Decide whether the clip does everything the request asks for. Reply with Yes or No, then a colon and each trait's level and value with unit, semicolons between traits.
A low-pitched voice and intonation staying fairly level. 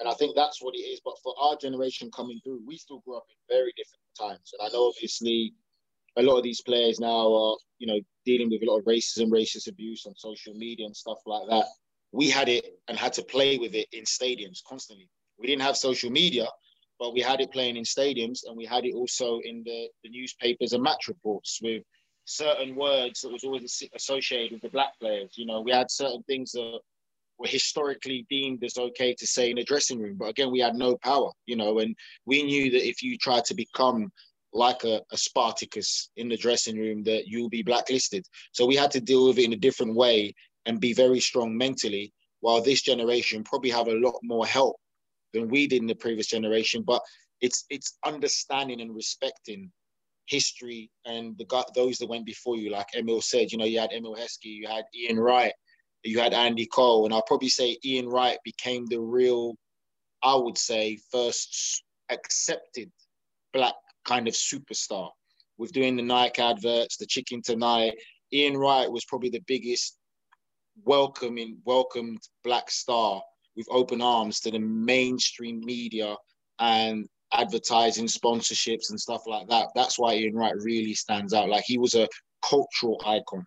Yes: low, 120 Hz; narrow, 2.3 semitones